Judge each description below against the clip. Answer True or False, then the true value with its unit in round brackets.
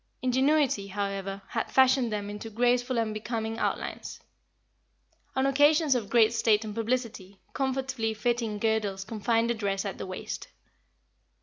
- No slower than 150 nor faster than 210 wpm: False (135 wpm)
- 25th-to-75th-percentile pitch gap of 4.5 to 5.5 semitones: False (3.4 semitones)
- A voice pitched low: False (225 Hz)